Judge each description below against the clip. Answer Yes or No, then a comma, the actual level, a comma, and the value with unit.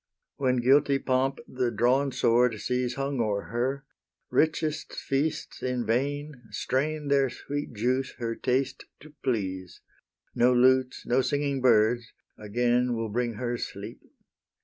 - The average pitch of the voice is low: Yes, low, 125 Hz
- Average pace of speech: No, slow, 130 wpm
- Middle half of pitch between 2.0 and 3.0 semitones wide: Yes, narrow, 2.4 semitones